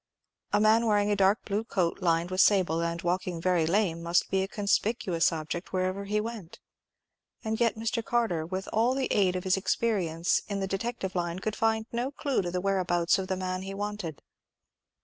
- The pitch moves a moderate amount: Yes, average, 3.5 semitones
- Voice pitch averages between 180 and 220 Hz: Yes, high, 190 Hz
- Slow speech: No, average, 195 wpm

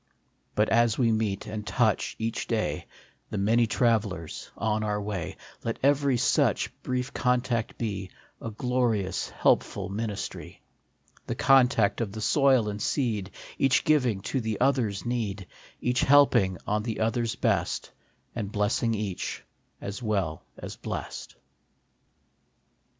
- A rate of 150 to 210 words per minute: No, slow, 135 wpm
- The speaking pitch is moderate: No, low, 110 Hz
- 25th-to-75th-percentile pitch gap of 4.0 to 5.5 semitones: No, average, 3.2 semitones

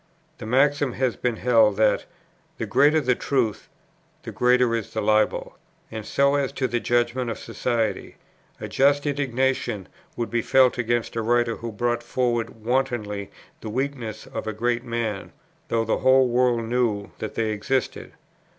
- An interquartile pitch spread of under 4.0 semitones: Yes, narrow, 2.6 semitones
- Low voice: Yes, low, 120 Hz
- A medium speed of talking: Yes, average, 160 wpm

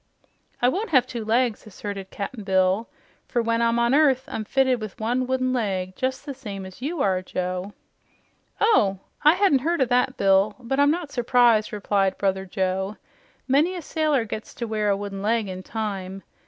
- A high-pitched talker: Yes, high, 230 Hz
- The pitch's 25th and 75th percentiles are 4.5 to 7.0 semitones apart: Yes, average, 4.9 semitones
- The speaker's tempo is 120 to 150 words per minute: No, average, 185 wpm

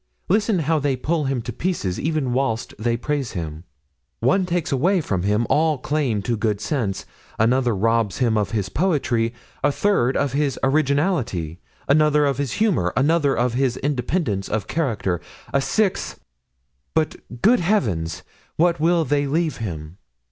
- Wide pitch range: Yes, wide, 6.4 semitones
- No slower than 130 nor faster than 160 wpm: Yes, average, 155 wpm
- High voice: No, low, 135 Hz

